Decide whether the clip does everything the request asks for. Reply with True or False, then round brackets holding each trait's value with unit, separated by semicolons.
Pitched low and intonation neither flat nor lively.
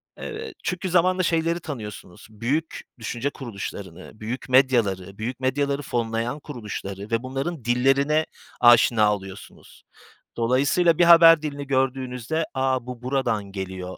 True (130 Hz; 4.6 semitones)